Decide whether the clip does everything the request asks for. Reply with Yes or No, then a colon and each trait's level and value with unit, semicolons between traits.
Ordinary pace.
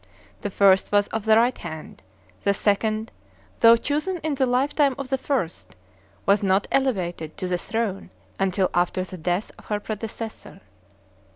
Yes: average, 160 wpm